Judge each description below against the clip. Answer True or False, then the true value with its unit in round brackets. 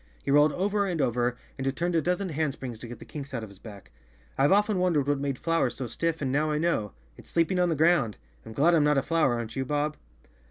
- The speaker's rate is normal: False (250 wpm)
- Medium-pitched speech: True (145 Hz)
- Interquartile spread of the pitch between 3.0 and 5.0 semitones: True (4.7 semitones)